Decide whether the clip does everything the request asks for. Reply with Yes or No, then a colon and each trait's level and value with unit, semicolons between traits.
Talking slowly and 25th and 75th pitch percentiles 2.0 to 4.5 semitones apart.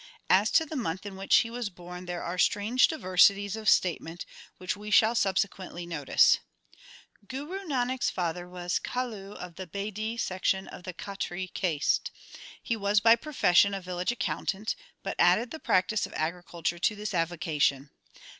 No: average, 170 wpm; average, 3.7 semitones